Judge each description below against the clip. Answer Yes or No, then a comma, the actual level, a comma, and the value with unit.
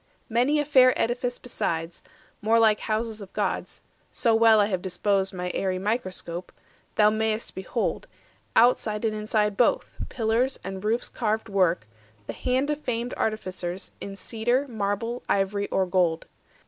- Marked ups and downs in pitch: No, average, 3.4 semitones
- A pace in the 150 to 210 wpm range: No, average, 140 wpm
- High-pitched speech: Yes, high, 215 Hz